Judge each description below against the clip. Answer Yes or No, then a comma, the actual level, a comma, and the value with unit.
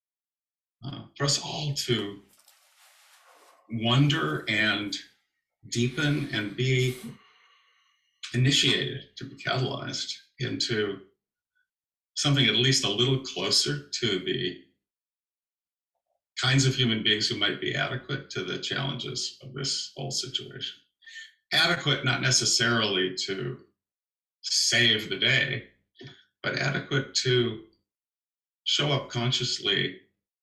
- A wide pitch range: No, average, 4.6 semitones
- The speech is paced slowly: Yes, slow, 100 wpm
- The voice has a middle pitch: No, low, 125 Hz